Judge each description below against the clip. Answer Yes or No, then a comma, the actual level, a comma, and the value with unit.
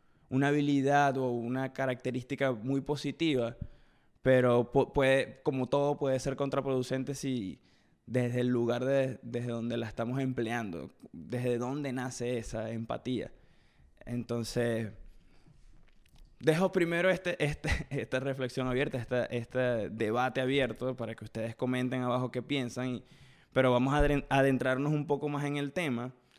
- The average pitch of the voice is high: No, low, 130 Hz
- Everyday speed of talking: Yes, average, 135 wpm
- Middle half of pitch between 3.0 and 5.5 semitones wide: No, narrow, 2.4 semitones